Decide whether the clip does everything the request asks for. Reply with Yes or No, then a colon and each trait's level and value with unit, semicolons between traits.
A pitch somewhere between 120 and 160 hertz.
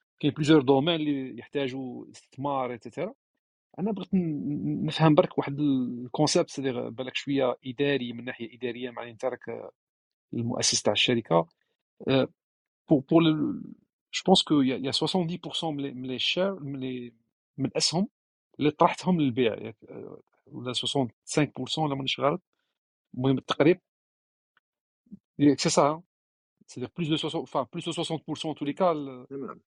Yes: medium, 140 Hz